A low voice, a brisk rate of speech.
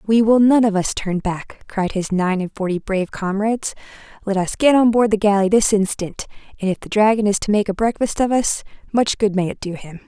No: high, 205 Hz; fast, 240 wpm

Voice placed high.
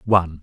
No: very low, 90 Hz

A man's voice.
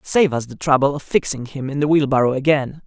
Yes: male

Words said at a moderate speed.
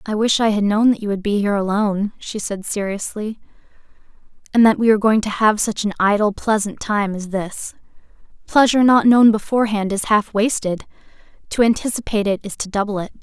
Yes: average, 190 wpm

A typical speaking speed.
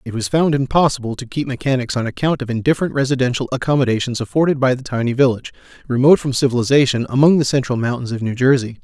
Yes: average, 190 wpm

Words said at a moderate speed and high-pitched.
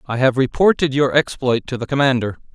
No: average, 190 wpm; low, 130 Hz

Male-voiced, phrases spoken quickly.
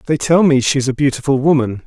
Yes: male; fast, 225 wpm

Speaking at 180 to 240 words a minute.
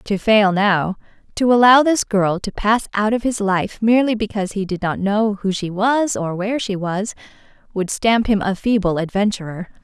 Yes: average, 195 wpm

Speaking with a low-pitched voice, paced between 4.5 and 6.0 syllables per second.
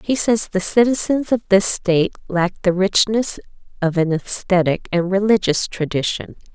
No: high, 195 Hz; 4.7 syllables/s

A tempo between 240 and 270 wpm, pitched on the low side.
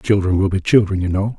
Yes: fast, 260 wpm; low, 100 Hz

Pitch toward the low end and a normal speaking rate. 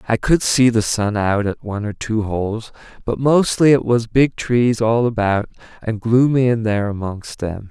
Yes: low, 115 Hz; average, 195 wpm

